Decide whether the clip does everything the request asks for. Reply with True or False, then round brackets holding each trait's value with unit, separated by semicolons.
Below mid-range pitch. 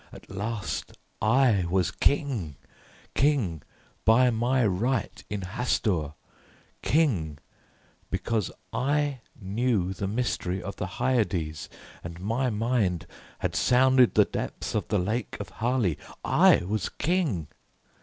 True (110 Hz)